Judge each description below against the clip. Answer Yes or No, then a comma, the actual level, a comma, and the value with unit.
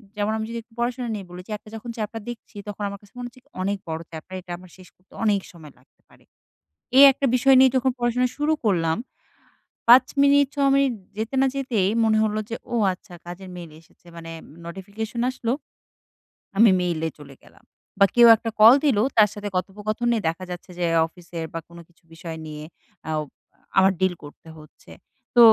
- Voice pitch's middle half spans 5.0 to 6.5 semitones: Yes, average, 5.3 semitones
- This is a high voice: Yes, high, 205 Hz